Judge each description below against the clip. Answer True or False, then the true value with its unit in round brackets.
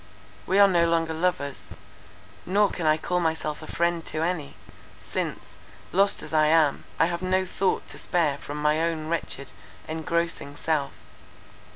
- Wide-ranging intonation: False (2.4 semitones)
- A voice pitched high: False (165 Hz)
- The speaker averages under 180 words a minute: True (160 wpm)